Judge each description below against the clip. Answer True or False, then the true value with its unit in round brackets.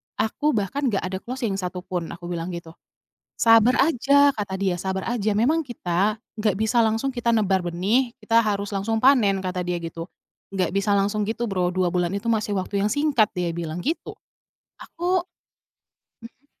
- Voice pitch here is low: False (205 Hz)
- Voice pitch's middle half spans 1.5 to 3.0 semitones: False (4.3 semitones)